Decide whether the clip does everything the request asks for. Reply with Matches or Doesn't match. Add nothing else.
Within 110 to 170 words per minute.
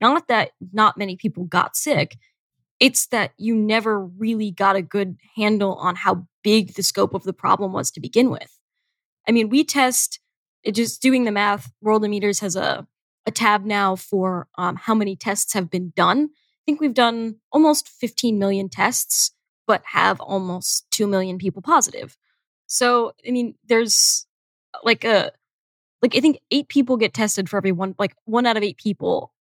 Doesn't match